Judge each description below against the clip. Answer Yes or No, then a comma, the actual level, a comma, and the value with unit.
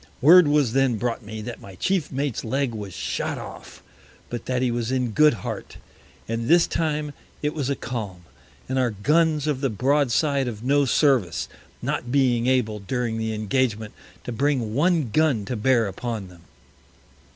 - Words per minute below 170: No, average, 175 wpm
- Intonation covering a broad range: No, average, 4.4 semitones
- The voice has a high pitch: No, low, 125 Hz